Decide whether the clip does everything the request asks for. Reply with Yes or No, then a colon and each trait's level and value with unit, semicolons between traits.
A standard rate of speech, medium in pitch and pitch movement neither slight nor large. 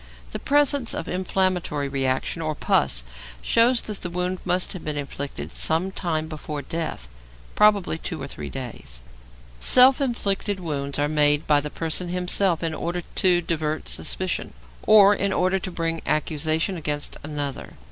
Yes: average, 155 wpm; medium, 165 Hz; average, 4.2 semitones